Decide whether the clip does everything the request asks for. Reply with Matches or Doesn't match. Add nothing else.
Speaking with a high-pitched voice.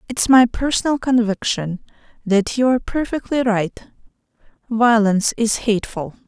Matches